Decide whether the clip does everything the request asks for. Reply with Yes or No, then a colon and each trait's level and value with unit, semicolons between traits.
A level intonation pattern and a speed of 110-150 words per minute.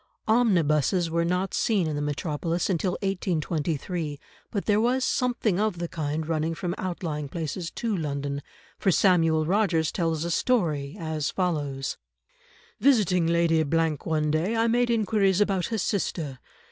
No: average, 4.1 semitones; average, 145 wpm